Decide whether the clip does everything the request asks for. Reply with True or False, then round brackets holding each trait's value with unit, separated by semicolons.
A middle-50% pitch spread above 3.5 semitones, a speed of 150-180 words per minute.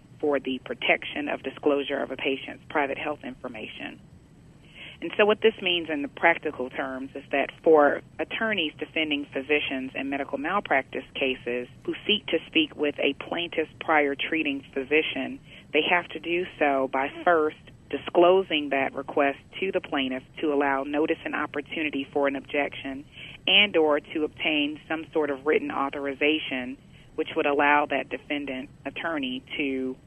False (2.8 semitones; 155 wpm)